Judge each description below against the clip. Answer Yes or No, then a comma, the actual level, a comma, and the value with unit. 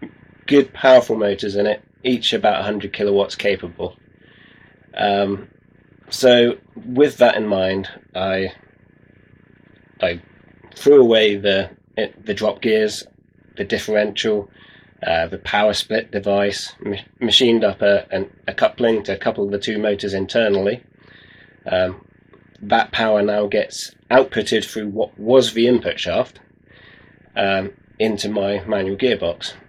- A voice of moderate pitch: No, low, 105 Hz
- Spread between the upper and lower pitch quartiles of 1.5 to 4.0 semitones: Yes, narrow, 2.4 semitones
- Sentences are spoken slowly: Yes, slow, 125 wpm